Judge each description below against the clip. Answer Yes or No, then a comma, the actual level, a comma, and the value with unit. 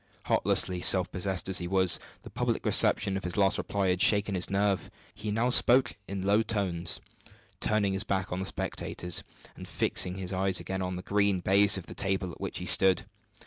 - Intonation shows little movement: Yes, narrow, 1.7 semitones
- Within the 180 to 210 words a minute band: Yes, average, 200 wpm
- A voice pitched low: Yes, very low, 95 Hz